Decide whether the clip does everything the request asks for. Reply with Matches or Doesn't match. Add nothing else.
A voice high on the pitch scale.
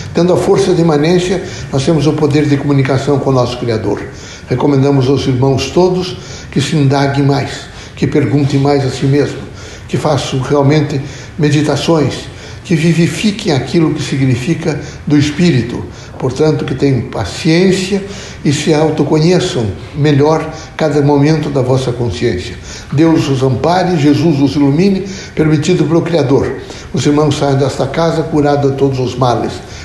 Doesn't match